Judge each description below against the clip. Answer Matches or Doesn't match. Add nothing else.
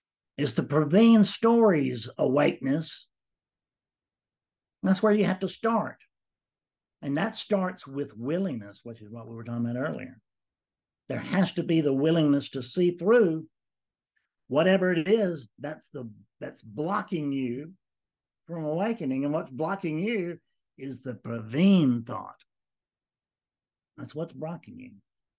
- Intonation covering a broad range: Matches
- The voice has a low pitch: Doesn't match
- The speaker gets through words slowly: Matches